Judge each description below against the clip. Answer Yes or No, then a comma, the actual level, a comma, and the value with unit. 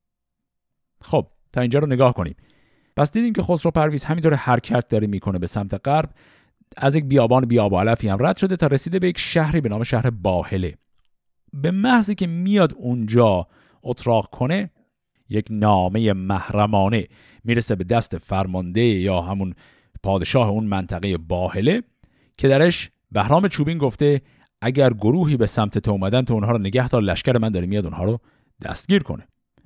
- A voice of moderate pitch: No, low, 120 Hz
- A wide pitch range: Yes, wide, 6.4 semitones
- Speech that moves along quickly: Yes, fast, 160 wpm